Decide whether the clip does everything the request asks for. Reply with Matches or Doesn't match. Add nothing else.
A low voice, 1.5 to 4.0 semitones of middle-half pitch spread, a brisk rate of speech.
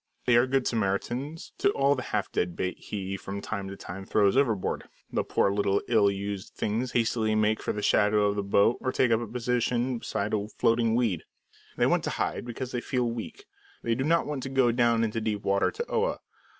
Matches